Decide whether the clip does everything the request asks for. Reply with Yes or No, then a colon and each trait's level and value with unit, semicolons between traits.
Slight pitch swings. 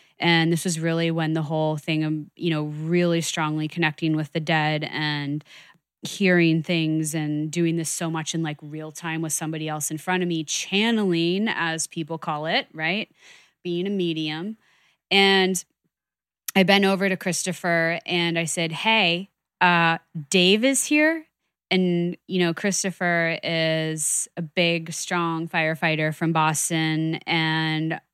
Yes: narrow, 2.1 semitones